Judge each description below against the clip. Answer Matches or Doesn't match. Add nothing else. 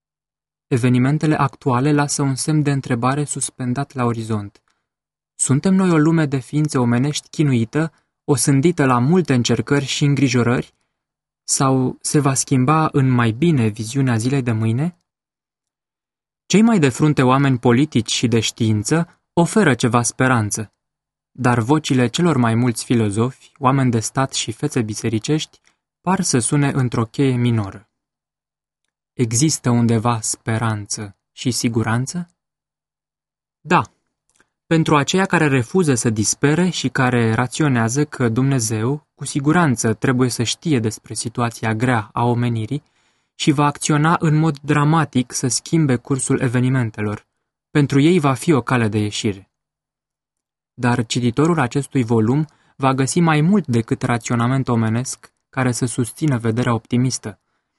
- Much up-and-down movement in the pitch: Doesn't match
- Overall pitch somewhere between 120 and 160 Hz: Matches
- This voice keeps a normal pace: Doesn't match